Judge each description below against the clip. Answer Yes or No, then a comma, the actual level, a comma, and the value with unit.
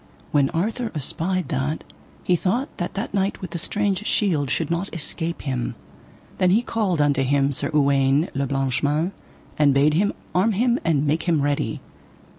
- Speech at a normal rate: Yes, average, 175 wpm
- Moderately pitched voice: Yes, medium, 165 Hz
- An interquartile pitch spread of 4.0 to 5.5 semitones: Yes, average, 5.1 semitones